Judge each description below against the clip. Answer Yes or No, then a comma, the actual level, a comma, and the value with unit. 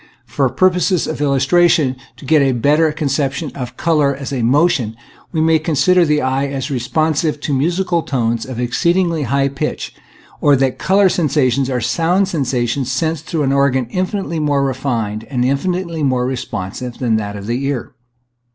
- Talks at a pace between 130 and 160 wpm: No, average, 170 wpm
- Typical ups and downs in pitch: Yes, average, 4.0 semitones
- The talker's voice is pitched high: No, medium, 140 Hz